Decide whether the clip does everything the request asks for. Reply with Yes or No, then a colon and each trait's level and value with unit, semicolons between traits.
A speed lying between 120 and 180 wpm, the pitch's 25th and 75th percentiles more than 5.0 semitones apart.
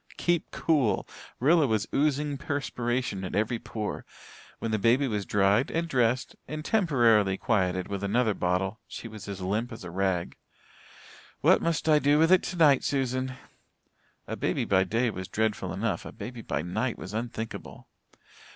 Yes: average, 160 wpm; wide, 5.5 semitones